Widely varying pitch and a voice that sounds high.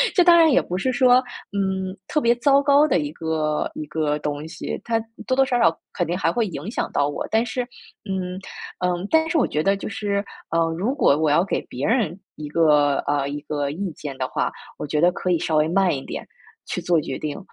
No: wide, 7.3 semitones; medium, 180 Hz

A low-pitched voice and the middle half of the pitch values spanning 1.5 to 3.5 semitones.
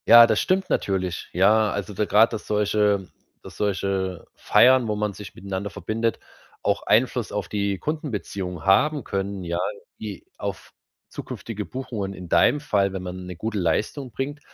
Yes: low, 105 Hz; average, 2.9 semitones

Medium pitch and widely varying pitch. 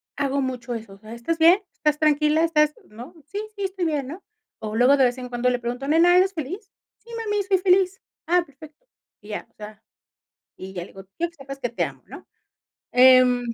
No: very high, 280 Hz; wide, 5.9 semitones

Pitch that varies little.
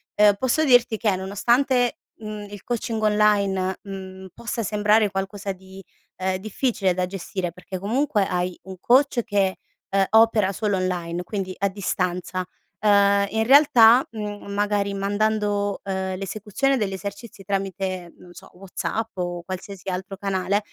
Yes: narrow, 2.3 semitones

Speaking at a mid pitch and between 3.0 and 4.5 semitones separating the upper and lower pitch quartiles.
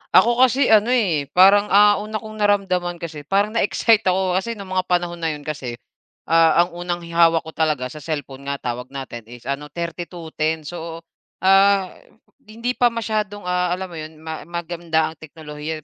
Yes: medium, 175 Hz; average, 4.2 semitones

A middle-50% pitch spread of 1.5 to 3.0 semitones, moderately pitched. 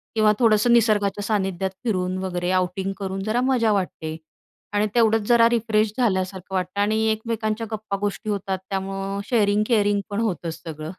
No: narrow, 2.4 semitones; high, 205 Hz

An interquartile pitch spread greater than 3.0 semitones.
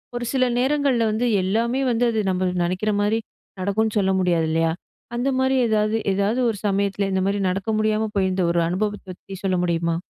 Yes: average, 3.4 semitones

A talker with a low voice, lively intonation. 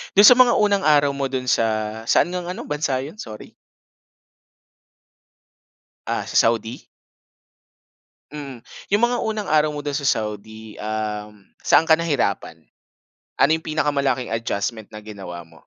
Yes: low, 130 Hz; wide, 6.3 semitones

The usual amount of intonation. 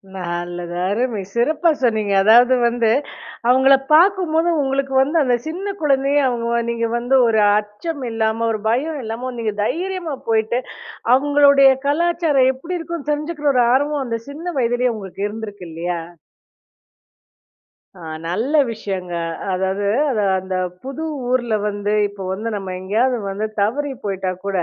No: wide, 5.7 semitones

